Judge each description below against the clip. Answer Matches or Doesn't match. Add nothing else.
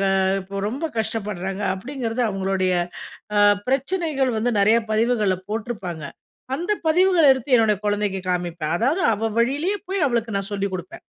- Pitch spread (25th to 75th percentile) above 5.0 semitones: Matches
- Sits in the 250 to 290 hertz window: Doesn't match